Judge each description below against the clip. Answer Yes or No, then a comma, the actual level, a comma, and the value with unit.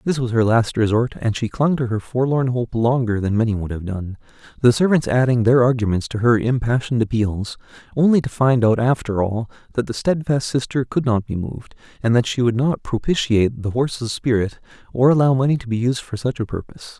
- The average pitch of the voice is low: Yes, low, 120 Hz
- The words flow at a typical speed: No, fast, 210 wpm